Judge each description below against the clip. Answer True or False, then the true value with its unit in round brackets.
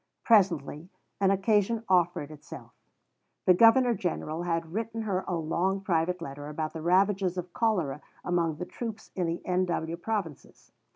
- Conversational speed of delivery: True (150 wpm)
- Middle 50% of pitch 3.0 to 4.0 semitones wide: True (3.3 semitones)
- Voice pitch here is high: False (180 Hz)